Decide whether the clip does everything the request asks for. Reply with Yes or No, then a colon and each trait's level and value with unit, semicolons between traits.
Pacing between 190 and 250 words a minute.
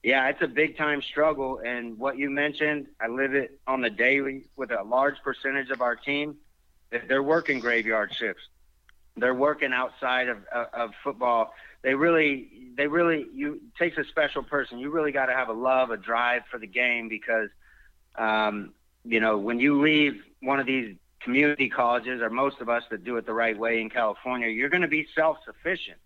Yes: average, 195 wpm